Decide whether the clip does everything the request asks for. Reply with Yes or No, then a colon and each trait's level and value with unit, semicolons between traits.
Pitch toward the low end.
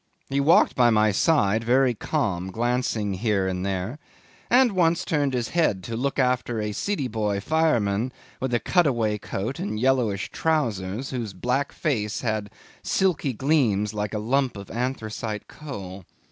Yes: low, 120 Hz